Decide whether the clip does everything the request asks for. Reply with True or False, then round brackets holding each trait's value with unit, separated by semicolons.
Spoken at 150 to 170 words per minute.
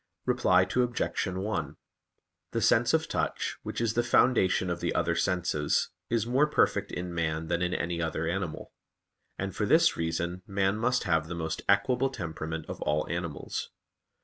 True (165 wpm)